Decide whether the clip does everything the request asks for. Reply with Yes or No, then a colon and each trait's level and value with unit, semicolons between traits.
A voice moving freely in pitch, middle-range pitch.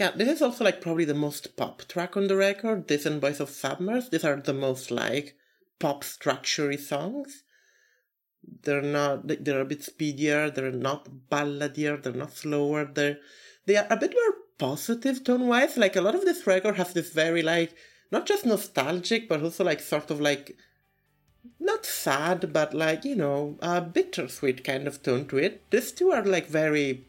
Yes: wide, 5.7 semitones; medium, 155 Hz